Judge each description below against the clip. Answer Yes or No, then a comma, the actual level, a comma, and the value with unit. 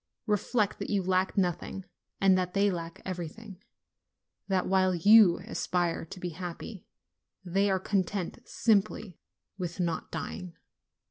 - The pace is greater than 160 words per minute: No, average, 145 wpm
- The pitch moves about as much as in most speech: No, narrow, 2.2 semitones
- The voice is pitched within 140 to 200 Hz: Yes, medium, 185 Hz